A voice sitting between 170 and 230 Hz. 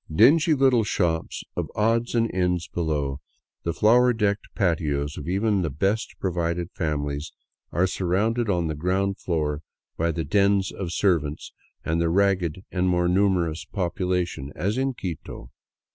No: very low, 90 Hz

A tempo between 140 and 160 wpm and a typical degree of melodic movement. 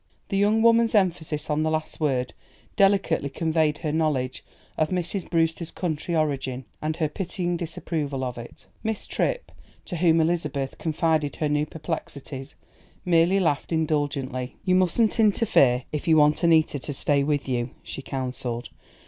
Yes: average, 150 wpm; average, 3.6 semitones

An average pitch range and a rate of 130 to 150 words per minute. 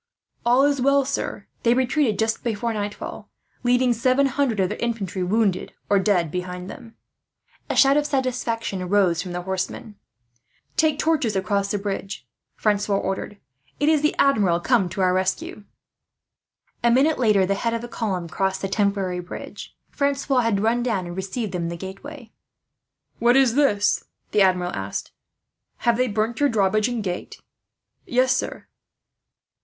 No: average, 4.7 semitones; average, 160 wpm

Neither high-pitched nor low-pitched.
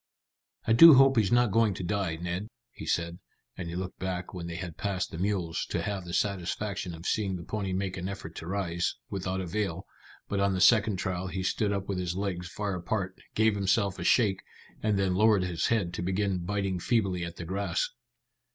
No: very low, 95 Hz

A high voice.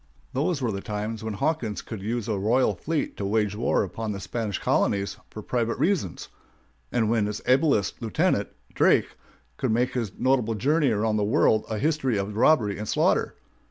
No: low, 110 Hz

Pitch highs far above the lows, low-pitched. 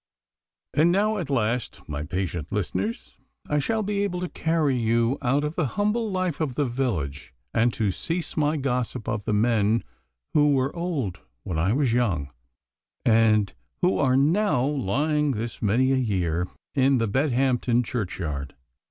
Yes: wide, 6.0 semitones; low, 125 Hz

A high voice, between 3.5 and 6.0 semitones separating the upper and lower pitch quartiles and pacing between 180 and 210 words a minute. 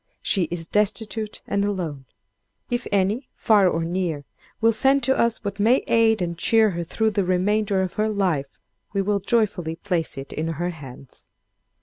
No: high, 195 Hz; average, 4.2 semitones; average, 170 wpm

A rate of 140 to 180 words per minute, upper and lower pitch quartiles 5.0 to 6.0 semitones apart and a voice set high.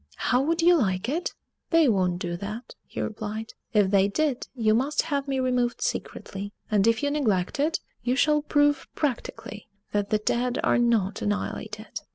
Yes: average, 175 wpm; wide, 5.6 semitones; high, 235 Hz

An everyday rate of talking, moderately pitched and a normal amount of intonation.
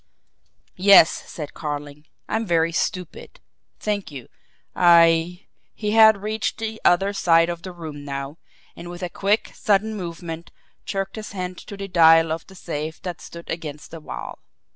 Yes: average, 165 wpm; medium, 175 Hz; average, 3.4 semitones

